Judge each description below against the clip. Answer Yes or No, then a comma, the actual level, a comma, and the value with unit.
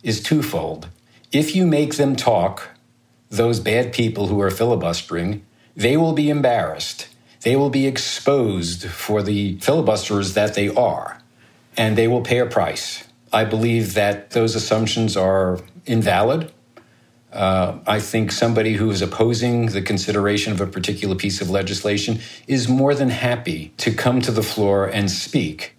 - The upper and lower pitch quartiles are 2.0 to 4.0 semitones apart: Yes, average, 3.1 semitones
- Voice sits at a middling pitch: No, low, 110 Hz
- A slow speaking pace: No, average, 155 wpm